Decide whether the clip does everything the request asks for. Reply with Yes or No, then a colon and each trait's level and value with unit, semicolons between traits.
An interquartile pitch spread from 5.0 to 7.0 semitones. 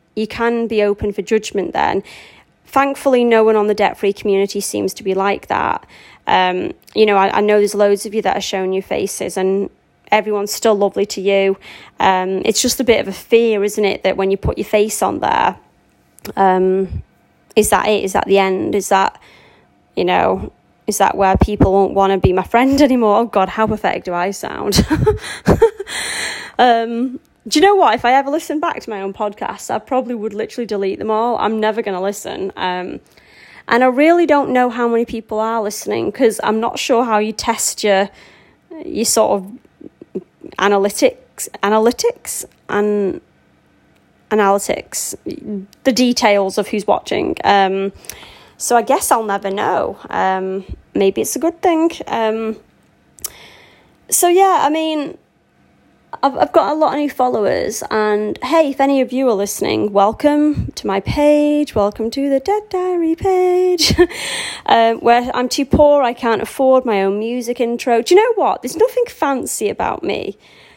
Yes: average, 5.3 semitones